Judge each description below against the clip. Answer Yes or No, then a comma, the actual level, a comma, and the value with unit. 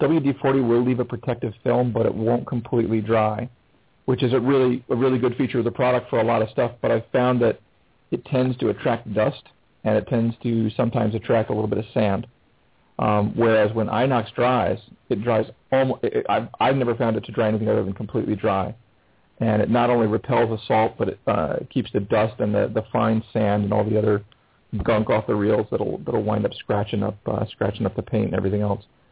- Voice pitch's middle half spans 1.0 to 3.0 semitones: Yes, narrow, 2.6 semitones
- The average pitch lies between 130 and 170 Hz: No, low, 115 Hz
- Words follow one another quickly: Yes, fast, 225 wpm